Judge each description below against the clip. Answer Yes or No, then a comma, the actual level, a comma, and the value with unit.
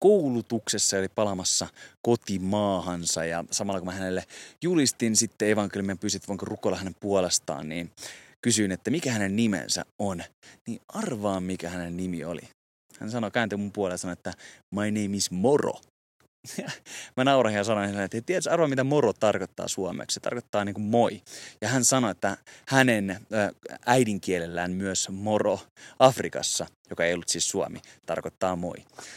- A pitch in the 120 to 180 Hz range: No, low, 100 Hz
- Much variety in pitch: No, average, 3.8 semitones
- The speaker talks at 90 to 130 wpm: No, average, 150 wpm